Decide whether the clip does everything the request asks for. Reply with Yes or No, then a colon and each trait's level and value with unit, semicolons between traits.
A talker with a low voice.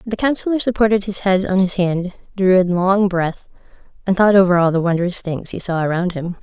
No: high, 190 Hz